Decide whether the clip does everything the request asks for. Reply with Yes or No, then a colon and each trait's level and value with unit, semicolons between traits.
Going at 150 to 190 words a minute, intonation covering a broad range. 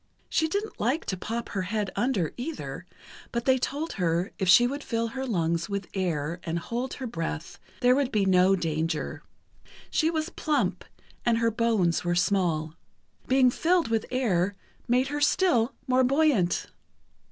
Yes: average, 165 wpm; wide, 6.7 semitones